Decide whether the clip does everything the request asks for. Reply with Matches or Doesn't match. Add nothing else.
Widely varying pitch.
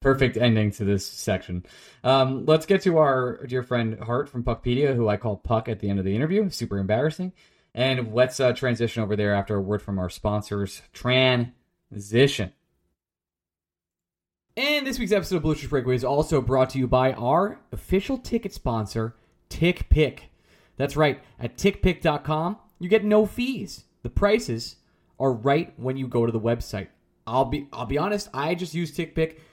Matches